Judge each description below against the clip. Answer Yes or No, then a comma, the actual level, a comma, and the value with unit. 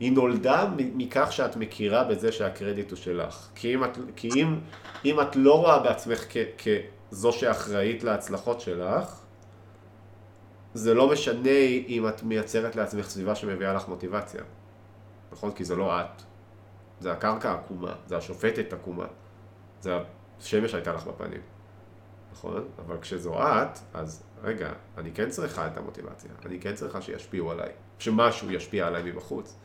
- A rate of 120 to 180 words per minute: Yes, average, 145 wpm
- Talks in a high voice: No, low, 105 Hz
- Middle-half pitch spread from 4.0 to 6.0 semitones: No, average, 3.1 semitones